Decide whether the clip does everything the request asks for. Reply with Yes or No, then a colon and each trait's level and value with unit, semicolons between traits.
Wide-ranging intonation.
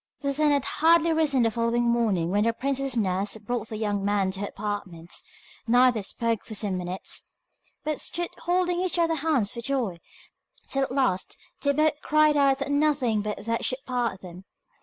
Yes: wide, 5.7 semitones